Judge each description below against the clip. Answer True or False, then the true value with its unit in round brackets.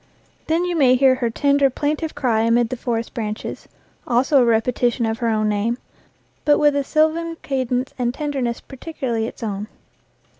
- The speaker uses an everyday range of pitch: True (3.7 semitones)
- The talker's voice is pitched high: True (250 Hz)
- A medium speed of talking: True (165 wpm)